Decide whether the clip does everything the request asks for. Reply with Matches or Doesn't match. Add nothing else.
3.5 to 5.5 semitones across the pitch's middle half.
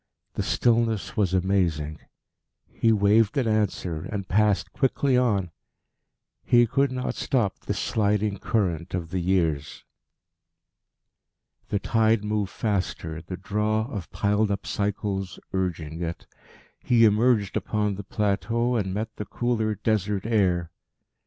Doesn't match